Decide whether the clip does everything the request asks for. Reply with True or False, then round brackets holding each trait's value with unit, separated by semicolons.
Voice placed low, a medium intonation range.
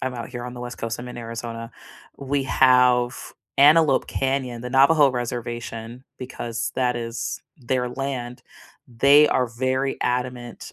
False (125 Hz; 1.8 semitones)